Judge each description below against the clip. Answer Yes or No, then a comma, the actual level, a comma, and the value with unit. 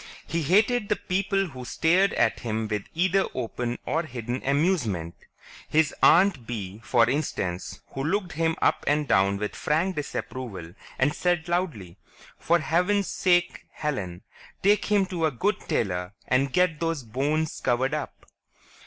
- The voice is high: No, medium, 150 Hz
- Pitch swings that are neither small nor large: No, wide, 7.1 semitones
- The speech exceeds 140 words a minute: Yes, average, 150 wpm